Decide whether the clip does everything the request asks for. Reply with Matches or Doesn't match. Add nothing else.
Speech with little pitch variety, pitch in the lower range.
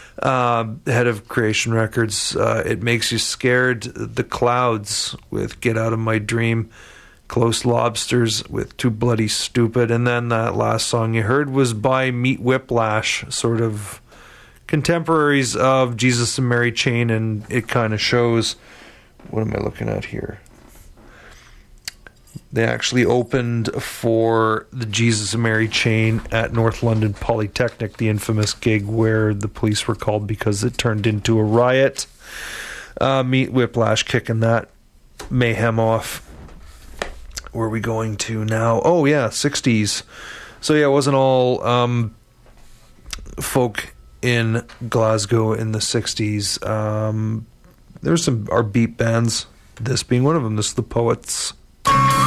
Matches